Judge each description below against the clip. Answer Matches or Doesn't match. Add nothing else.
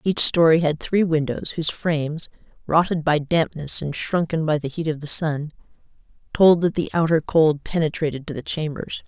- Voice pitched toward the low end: Doesn't match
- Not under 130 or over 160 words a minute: Doesn't match